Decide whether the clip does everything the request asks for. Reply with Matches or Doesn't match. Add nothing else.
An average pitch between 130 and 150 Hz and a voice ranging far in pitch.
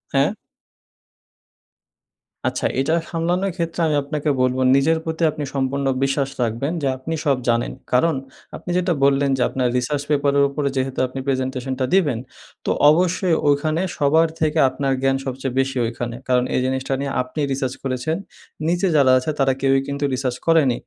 Doesn't match